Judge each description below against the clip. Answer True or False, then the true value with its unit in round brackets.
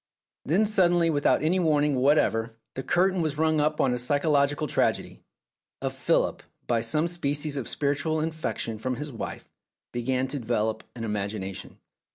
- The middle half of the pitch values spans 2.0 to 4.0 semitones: False (4.6 semitones)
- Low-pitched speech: False (145 Hz)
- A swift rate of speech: False (155 wpm)